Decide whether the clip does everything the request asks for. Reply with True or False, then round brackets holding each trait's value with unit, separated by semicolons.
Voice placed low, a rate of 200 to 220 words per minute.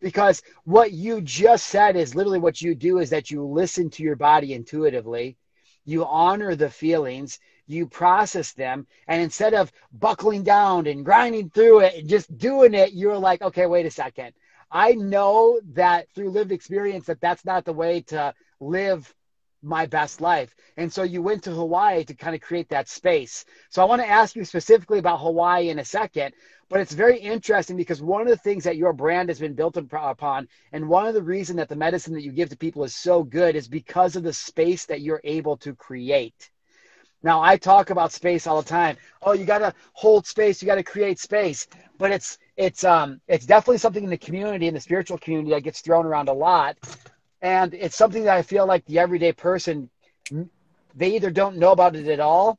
False (175 Hz; 205 wpm)